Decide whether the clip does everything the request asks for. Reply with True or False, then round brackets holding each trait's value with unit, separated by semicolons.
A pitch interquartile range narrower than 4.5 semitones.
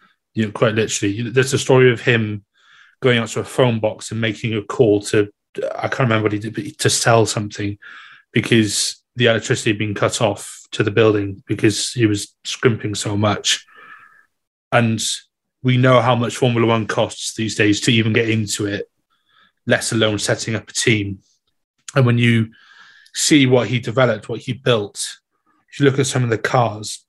True (3.0 semitones)